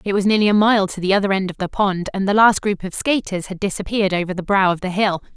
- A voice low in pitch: No, high, 195 Hz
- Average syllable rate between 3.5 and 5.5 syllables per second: No, 6.5 syllables/s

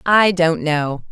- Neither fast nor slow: Yes, average, 160 wpm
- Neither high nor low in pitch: Yes, medium, 165 Hz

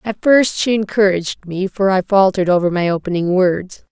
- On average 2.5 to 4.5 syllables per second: No, 5.4 syllables/s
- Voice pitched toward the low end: No, high, 190 Hz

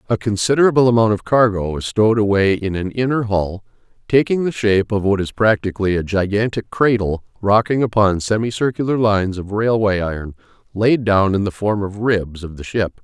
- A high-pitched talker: No, low, 105 Hz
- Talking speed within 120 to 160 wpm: No, average, 180 wpm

